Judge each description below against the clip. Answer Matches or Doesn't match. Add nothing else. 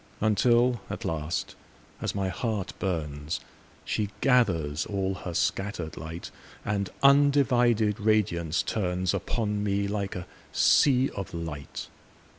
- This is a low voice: Matches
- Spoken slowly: Matches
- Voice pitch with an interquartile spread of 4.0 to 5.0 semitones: Matches